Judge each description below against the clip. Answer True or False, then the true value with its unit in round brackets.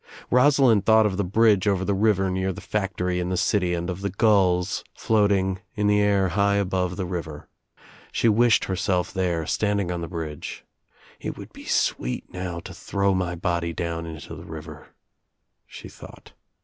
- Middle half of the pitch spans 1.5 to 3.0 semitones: True (2.5 semitones)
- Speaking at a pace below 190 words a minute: True (175 wpm)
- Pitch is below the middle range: True (95 Hz)